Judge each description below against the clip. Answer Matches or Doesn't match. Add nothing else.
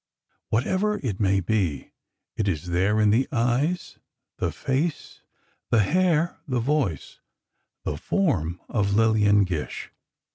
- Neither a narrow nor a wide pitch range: Doesn't match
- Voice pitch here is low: Matches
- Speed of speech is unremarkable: Doesn't match